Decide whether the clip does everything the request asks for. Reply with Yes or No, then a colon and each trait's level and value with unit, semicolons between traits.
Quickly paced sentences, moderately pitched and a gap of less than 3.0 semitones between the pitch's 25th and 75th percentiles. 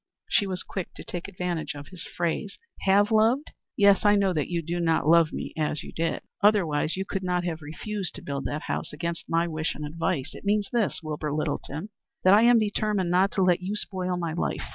No: fast, 220 wpm; medium, 180 Hz; average, 3.9 semitones